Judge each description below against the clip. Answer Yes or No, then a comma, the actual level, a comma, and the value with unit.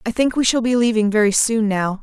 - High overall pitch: Yes, high, 220 Hz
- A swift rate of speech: Yes, fast, 265 wpm